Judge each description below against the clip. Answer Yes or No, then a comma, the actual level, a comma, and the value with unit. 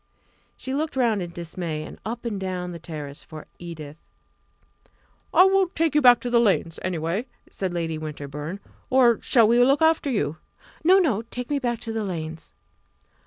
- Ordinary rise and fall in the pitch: No, wide, 7.4 semitones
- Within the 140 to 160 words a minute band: No, average, 175 wpm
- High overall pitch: Yes, high, 200 Hz